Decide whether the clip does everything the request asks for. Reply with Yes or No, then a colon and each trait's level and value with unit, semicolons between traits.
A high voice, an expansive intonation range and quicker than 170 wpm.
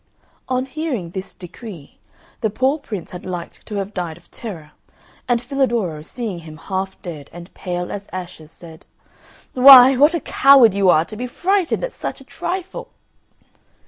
No: high, 200 Hz; wide, 6.7 semitones; average, 165 wpm